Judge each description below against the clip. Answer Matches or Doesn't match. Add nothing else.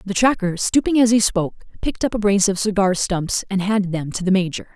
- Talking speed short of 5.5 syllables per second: Doesn't match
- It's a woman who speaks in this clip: Matches